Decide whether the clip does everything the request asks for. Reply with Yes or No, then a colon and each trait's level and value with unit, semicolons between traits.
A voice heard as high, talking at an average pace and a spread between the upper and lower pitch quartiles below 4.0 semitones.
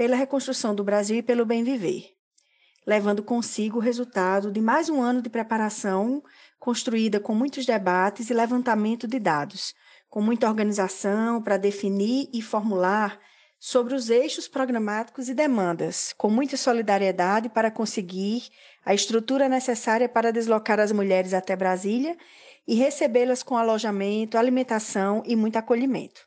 Yes: high, 225 Hz; average, 140 wpm; average, 3.1 semitones